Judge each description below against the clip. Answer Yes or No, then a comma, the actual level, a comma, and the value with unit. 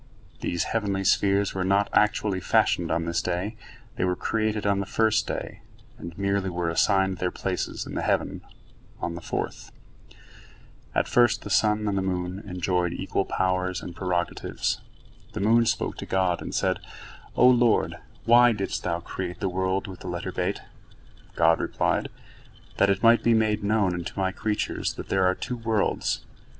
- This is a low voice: Yes, very low, 95 Hz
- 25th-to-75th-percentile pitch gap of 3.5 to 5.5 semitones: No, average, 2.9 semitones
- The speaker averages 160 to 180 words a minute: Yes, average, 170 wpm